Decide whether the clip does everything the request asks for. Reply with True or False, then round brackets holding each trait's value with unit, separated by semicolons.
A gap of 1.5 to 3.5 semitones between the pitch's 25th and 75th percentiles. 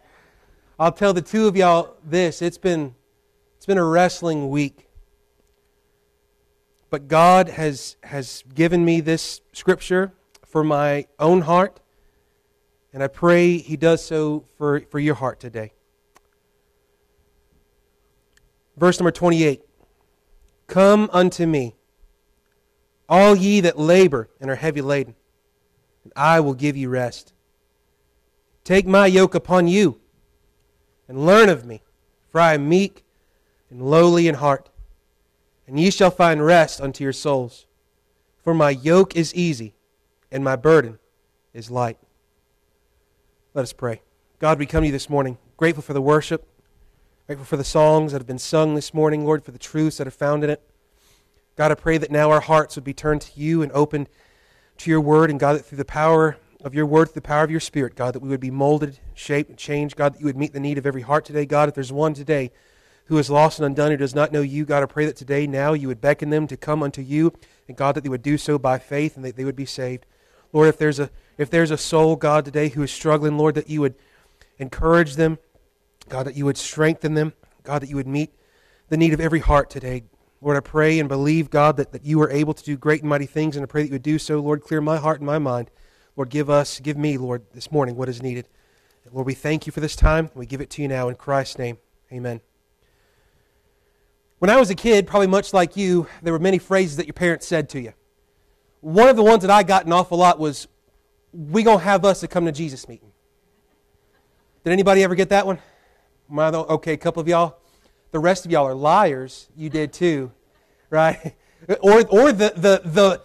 True (3.2 semitones)